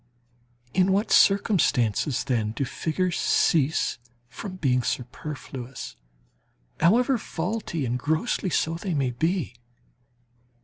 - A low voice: No, medium, 160 Hz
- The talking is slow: Yes, slow, 100 wpm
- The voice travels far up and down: Yes, wide, 6.7 semitones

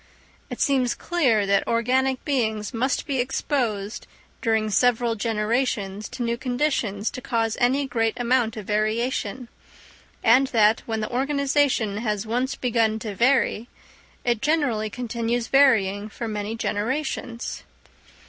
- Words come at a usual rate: No, slow, 130 wpm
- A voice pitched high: Yes, high, 235 Hz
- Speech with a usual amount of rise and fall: Yes, average, 3.1 semitones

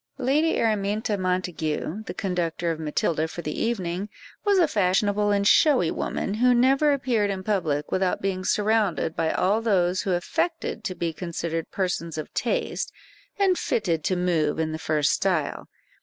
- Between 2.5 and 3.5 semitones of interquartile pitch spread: No, average, 4.5 semitones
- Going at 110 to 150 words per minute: No, average, 160 wpm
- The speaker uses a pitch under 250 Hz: Yes, high, 190 Hz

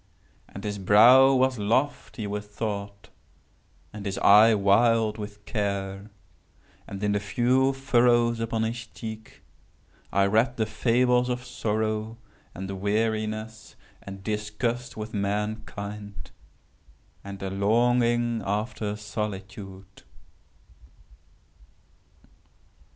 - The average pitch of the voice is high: No, low, 110 Hz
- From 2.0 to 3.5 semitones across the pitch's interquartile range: Yes, narrow, 2.5 semitones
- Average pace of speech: No, slow, 100 wpm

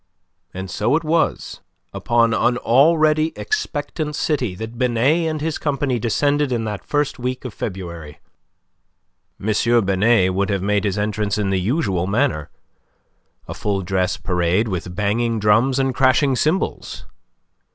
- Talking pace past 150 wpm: No, average, 140 wpm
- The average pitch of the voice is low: Yes, low, 115 Hz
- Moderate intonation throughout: No, wide, 6.3 semitones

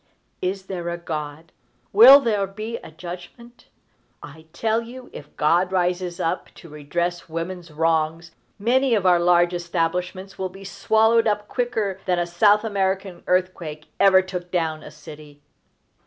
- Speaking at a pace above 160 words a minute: No, average, 155 wpm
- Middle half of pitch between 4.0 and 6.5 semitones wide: No, average, 3.2 semitones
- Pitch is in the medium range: Yes, medium, 180 Hz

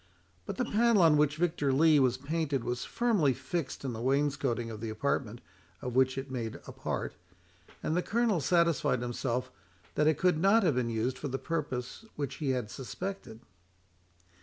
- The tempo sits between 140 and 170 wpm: No, average, 180 wpm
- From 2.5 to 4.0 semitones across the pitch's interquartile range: No, average, 5.0 semitones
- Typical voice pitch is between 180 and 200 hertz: No, medium, 140 Hz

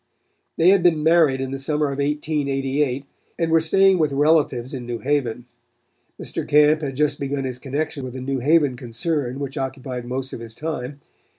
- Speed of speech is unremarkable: Yes, average, 185 wpm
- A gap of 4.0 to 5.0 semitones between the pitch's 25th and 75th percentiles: No, average, 2.8 semitones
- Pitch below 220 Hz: Yes, medium, 140 Hz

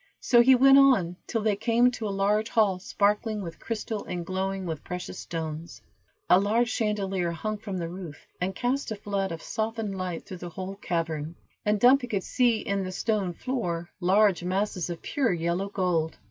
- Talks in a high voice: Yes, high, 195 Hz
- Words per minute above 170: Yes, average, 190 wpm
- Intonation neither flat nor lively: Yes, average, 3.7 semitones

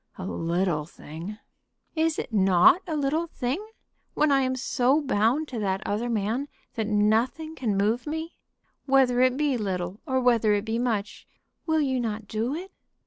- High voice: Yes, high, 240 Hz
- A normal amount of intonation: Yes, average, 5.0 semitones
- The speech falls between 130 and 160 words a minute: No, average, 170 wpm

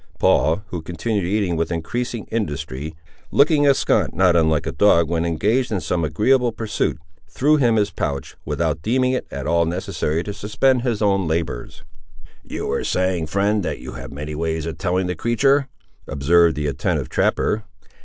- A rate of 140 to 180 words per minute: Yes, average, 170 wpm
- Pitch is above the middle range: No, very low, 90 Hz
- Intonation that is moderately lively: No, wide, 5.7 semitones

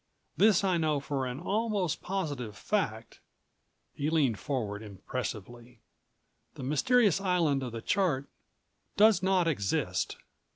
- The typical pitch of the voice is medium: Yes, medium, 145 Hz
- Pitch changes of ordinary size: No, wide, 7.7 semitones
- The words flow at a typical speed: No, slow, 120 wpm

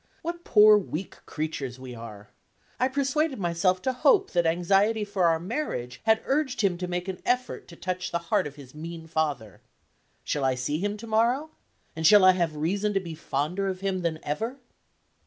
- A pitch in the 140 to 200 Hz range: Yes, medium, 185 Hz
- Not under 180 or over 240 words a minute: Yes, average, 195 wpm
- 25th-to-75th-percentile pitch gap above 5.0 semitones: Yes, wide, 5.5 semitones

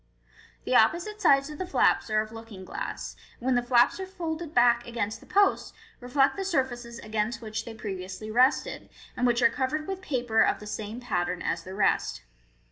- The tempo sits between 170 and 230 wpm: Yes, average, 195 wpm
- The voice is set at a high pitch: Yes, high, 240 Hz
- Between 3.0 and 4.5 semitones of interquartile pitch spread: No, average, 5.1 semitones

